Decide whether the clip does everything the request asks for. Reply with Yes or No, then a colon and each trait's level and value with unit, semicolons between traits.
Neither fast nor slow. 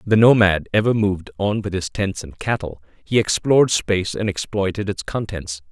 Yes: average, 180 wpm